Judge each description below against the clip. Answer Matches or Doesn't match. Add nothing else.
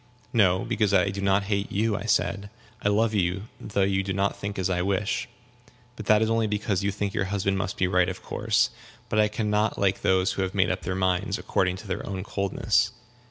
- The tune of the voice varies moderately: Doesn't match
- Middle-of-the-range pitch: Doesn't match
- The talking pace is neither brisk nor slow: Doesn't match